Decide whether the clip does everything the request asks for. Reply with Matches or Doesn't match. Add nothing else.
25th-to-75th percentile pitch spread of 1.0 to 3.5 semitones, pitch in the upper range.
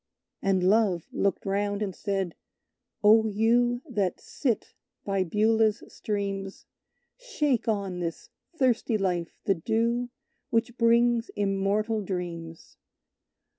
Matches